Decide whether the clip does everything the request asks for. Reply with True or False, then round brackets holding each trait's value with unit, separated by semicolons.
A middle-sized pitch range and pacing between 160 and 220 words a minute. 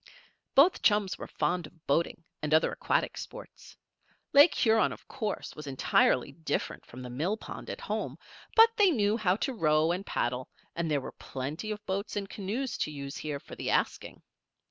False (6.2 semitones; 180 wpm)